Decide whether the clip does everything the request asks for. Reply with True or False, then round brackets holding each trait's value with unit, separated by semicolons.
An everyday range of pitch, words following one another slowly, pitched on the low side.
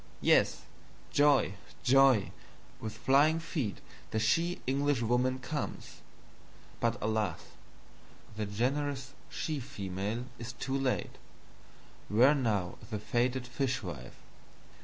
True (3.9 semitones; 100 wpm; 125 Hz)